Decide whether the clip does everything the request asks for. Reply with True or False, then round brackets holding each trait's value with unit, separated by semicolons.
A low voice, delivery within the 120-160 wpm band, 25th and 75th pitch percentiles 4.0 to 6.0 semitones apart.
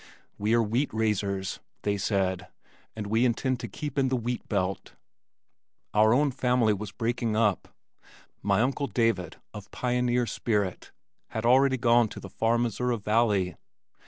False (115 Hz; 155 wpm; 3.2 semitones)